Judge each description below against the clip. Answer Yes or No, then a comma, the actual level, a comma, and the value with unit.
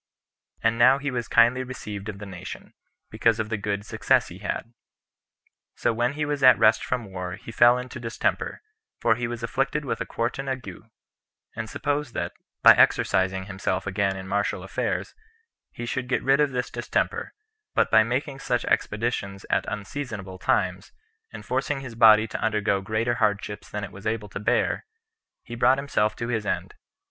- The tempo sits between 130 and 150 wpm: No, average, 180 wpm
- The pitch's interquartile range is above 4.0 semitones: No, average, 3.6 semitones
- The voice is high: No, low, 115 Hz